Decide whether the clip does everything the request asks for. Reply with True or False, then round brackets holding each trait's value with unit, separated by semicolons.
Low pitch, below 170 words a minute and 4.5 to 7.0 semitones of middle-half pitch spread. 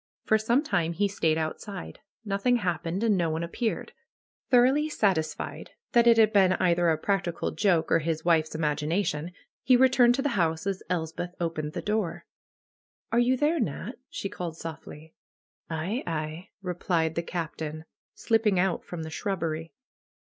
False (175 Hz; 155 wpm; 4.9 semitones)